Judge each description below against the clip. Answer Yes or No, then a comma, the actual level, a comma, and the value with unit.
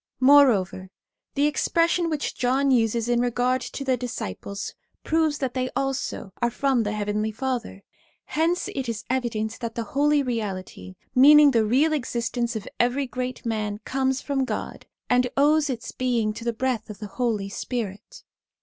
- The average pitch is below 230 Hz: No, high, 245 Hz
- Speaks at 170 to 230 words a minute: No, average, 160 wpm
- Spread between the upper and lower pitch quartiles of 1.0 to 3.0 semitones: No, average, 3.7 semitones